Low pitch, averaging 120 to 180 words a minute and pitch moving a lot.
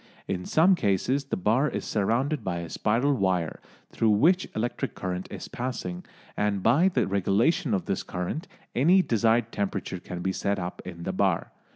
Yes: low, 105 Hz; average, 175 wpm; wide, 6.2 semitones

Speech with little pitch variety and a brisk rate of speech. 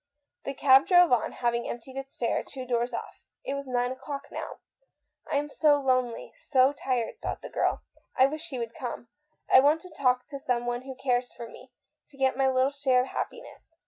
Yes: narrow, 2.1 semitones; fast, 215 wpm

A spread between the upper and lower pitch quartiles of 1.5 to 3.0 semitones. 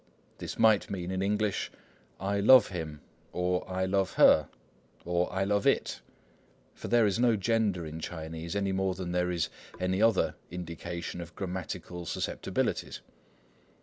Yes: narrow, 2.6 semitones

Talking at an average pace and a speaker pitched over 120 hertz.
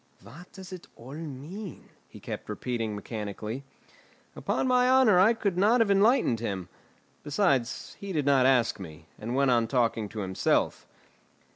Yes: average, 160 wpm; low, 135 Hz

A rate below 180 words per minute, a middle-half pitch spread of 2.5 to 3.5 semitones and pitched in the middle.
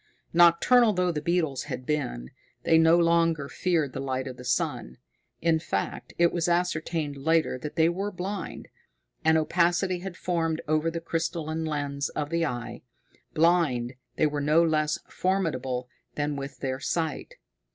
Yes: average, 155 wpm; average, 3.2 semitones; medium, 160 Hz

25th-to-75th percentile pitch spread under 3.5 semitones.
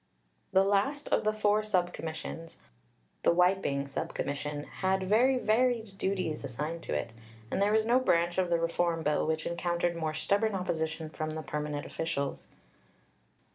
No: average, 4.3 semitones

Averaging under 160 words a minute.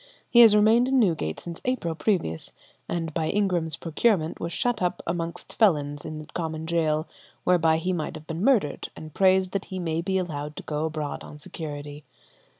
No: average, 185 wpm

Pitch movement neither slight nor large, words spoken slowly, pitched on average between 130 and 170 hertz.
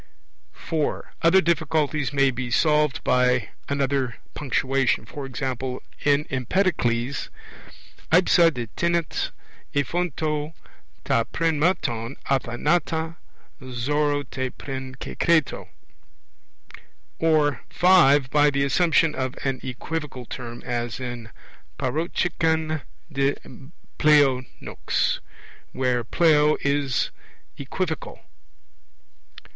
Yes: average, 3.7 semitones; slow, 85 wpm; medium, 140 Hz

